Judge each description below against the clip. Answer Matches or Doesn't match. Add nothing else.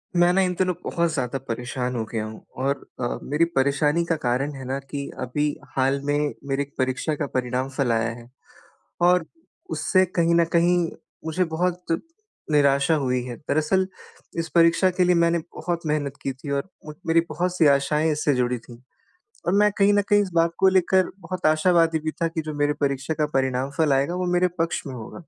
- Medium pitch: Matches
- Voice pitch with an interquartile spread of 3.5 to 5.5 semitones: Matches